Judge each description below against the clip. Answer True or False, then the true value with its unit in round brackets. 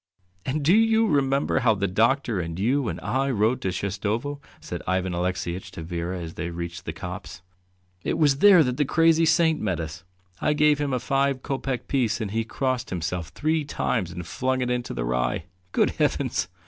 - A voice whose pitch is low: True (120 Hz)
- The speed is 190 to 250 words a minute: True (195 wpm)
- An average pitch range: False (7.5 semitones)